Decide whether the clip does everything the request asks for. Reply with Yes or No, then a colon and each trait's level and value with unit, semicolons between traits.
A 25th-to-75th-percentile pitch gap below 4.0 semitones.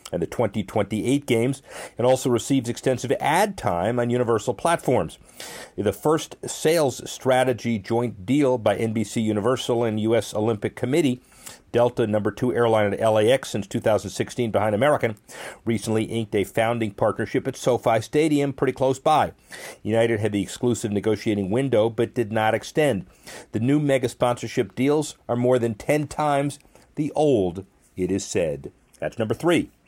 Yes: average, 2.9 semitones